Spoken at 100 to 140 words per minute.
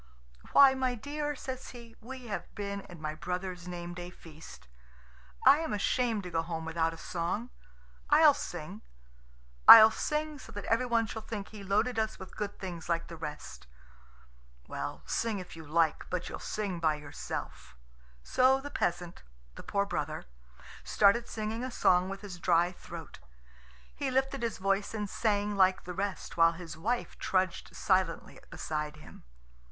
No: average, 165 wpm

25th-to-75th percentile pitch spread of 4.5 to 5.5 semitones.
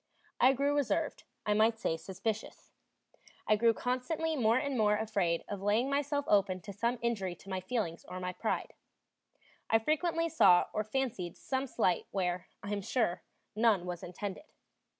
Yes: average, 5.2 semitones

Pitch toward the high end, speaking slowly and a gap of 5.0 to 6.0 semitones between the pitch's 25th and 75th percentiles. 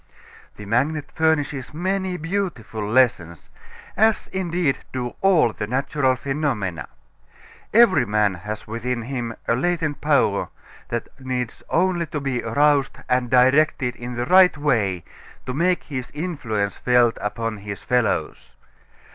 No: low, 130 Hz; slow, 130 wpm; average, 5.3 semitones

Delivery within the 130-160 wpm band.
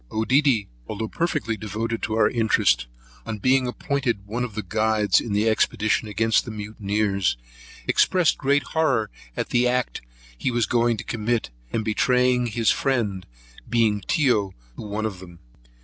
Yes: average, 155 wpm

